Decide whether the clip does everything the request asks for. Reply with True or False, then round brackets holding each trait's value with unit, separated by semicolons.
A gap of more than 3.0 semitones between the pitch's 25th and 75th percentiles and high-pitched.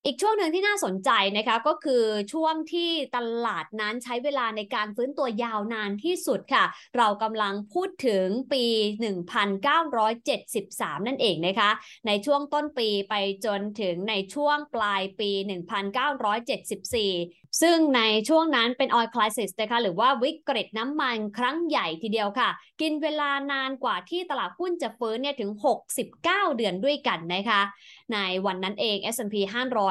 True (5.5 semitones; 230 Hz)